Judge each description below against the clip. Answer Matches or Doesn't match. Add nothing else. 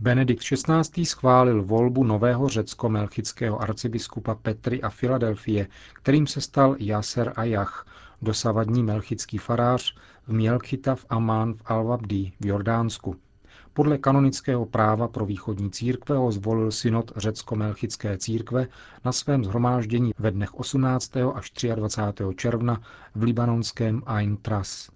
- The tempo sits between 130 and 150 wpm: Doesn't match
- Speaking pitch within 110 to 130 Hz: Matches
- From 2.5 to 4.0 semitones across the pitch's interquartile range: Matches